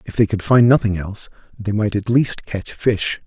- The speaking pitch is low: Yes, low, 110 Hz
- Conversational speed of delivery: No, fast, 220 wpm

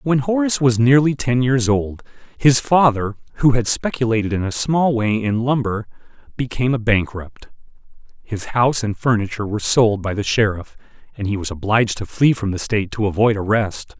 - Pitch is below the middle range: Yes, low, 115 Hz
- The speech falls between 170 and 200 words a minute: Yes, average, 180 wpm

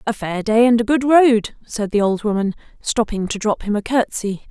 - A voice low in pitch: No, high, 220 Hz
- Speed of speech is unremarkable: No, fast, 225 wpm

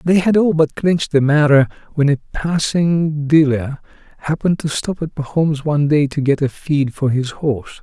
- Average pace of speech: Yes, average, 190 wpm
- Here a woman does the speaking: No, male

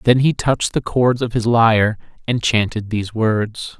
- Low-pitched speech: Yes, low, 115 Hz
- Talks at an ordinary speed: Yes, average, 190 wpm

